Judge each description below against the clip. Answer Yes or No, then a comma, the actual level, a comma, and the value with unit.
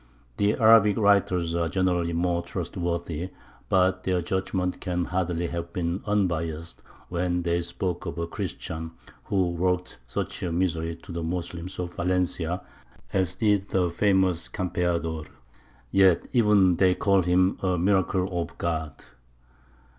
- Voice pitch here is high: No, very low, 90 Hz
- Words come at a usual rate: No, slow, 130 wpm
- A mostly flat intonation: Yes, narrow, 1.8 semitones